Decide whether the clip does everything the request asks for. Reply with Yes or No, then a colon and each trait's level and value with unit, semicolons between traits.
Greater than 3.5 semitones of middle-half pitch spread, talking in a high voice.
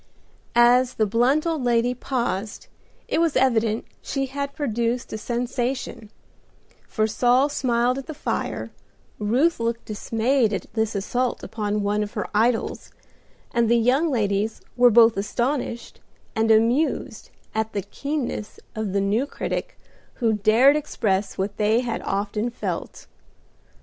No: average, 3.0 semitones; high, 235 Hz